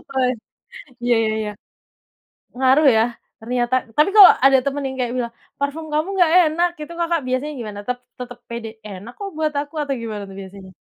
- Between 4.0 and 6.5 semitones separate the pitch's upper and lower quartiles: Yes, average, 4.5 semitones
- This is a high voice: Yes, very high, 255 Hz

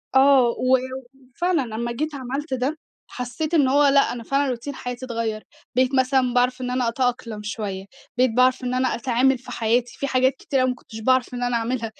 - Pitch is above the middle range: Yes, very high, 255 Hz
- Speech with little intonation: Yes, narrow, 1.8 semitones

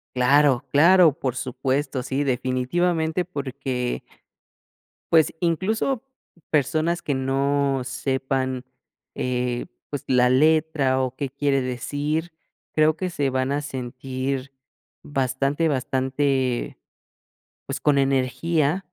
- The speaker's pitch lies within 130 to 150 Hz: Yes, low, 135 Hz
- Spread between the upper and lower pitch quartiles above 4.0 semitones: No, average, 2.8 semitones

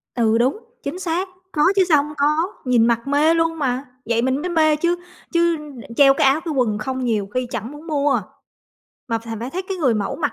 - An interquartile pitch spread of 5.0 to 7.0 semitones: Yes, average, 5.3 semitones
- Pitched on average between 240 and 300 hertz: Yes, very high, 280 Hz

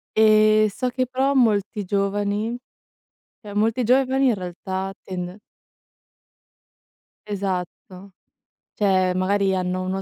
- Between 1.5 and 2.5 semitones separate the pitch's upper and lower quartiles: No, average, 2.9 semitones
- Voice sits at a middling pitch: No, high, 205 Hz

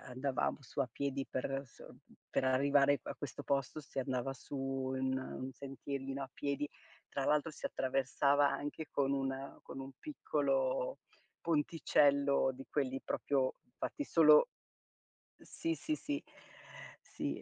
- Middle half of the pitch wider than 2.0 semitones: No, narrow, 1.7 semitones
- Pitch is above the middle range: No, medium, 140 Hz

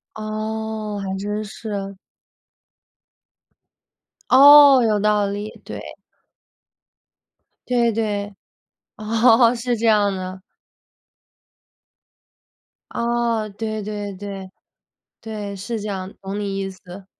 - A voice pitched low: No, high, 210 Hz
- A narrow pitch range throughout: Yes, narrow, 2.0 semitones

